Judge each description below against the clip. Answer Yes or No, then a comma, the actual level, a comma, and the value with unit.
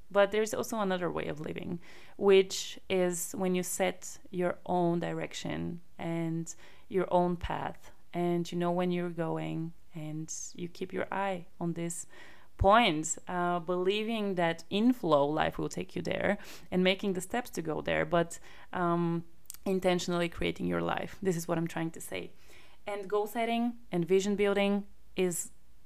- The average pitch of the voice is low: No, medium, 180 Hz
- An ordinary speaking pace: Yes, average, 160 wpm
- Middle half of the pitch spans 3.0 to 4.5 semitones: No, narrow, 2.5 semitones